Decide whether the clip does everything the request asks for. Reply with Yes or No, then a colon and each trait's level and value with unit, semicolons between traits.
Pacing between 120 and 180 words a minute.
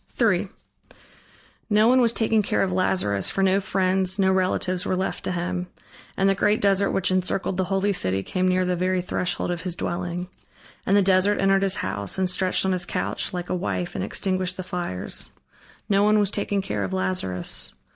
No: average, 195 wpm